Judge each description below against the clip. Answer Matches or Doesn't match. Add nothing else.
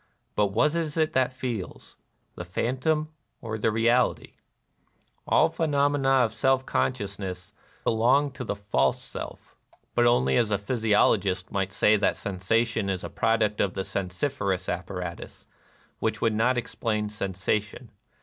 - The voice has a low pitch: Matches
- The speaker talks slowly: Doesn't match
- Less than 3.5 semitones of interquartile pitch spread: Doesn't match